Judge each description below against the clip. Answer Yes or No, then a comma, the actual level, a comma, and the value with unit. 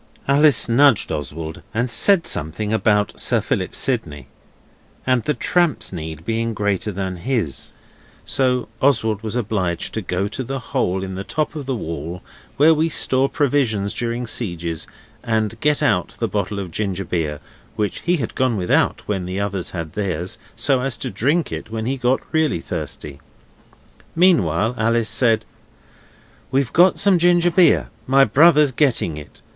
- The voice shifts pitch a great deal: Yes, wide, 6.4 semitones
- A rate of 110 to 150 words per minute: No, average, 160 wpm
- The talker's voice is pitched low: Yes, low, 110 Hz